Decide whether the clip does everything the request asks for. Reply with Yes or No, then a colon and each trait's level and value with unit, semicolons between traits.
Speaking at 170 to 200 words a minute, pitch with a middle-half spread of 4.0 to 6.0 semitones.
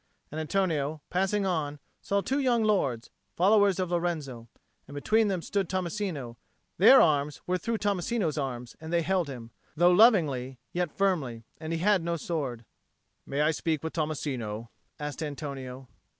No: average, 155 wpm; average, 5.3 semitones